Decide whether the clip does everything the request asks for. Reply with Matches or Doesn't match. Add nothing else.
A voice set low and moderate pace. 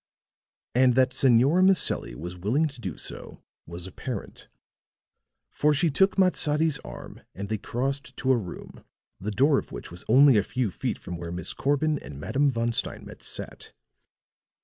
Matches